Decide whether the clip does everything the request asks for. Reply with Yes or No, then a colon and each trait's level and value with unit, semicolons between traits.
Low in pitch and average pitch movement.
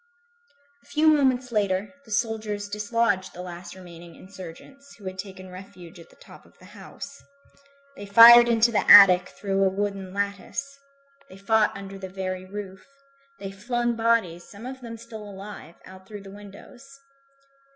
No: high, 200 Hz; average, 3.5 semitones